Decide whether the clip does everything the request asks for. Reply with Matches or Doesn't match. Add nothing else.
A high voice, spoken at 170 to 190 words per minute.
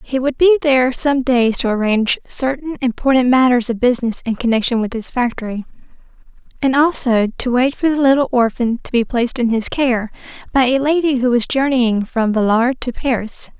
Matches